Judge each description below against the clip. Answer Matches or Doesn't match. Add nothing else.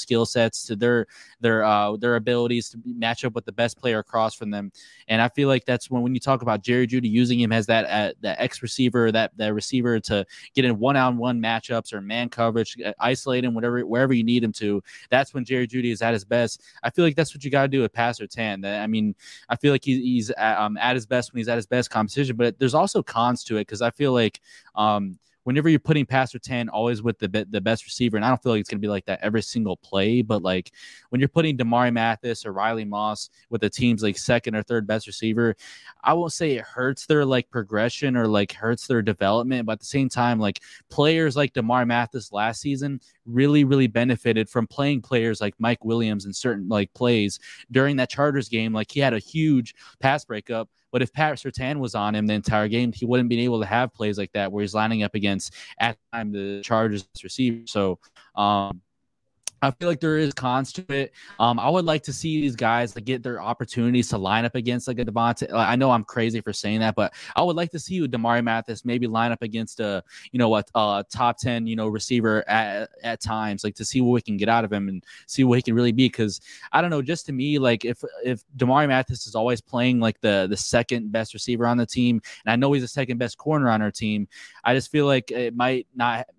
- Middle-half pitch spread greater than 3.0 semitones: Doesn't match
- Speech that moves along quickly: Matches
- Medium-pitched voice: Doesn't match